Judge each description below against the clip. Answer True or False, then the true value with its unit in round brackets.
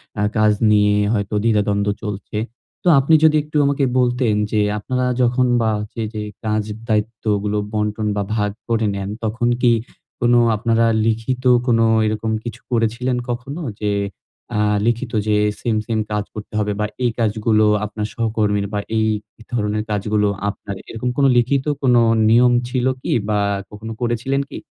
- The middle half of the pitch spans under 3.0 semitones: True (2.4 semitones)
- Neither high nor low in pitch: False (110 Hz)